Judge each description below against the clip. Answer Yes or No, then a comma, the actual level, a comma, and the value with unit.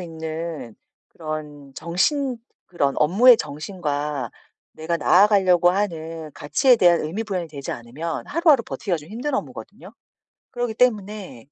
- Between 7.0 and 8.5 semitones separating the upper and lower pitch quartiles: No, wide, 5.5 semitones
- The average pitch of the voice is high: No, medium, 170 Hz